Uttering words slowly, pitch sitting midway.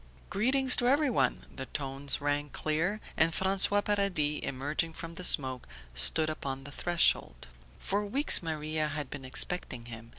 No: average, 145 wpm; medium, 155 Hz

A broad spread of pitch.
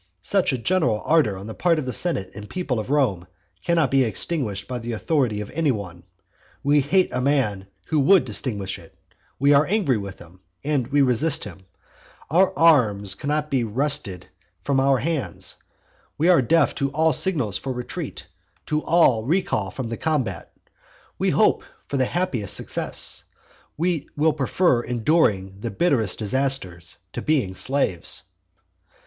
Yes: wide, 6.4 semitones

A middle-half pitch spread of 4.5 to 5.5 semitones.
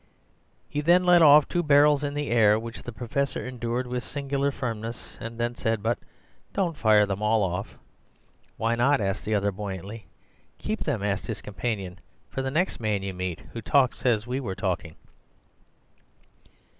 Yes: average, 5.0 semitones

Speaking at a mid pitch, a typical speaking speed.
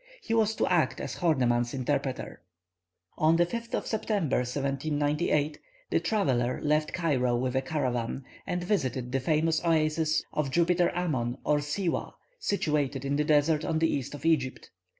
Yes: medium, 150 Hz; average, 155 wpm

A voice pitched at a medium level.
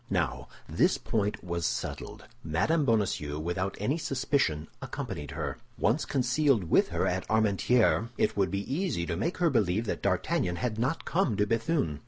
No: low, 105 Hz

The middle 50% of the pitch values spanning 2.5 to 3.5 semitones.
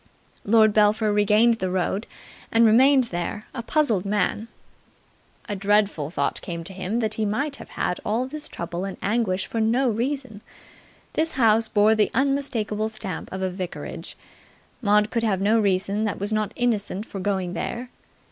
Yes: average, 2.9 semitones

